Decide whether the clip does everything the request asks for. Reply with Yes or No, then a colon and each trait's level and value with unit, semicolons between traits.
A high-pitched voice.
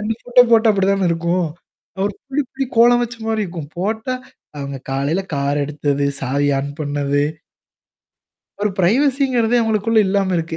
Yes: high, 195 Hz